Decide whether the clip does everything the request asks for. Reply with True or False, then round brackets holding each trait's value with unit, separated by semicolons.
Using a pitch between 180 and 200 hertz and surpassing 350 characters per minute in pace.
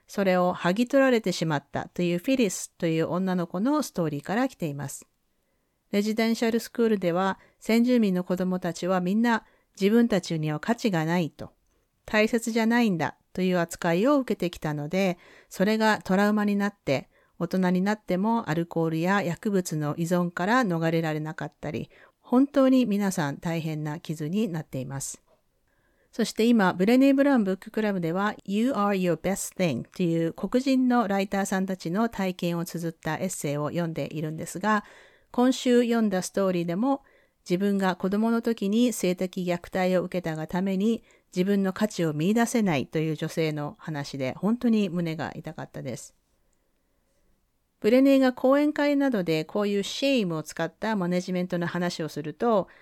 True (185 Hz; 370 characters per minute)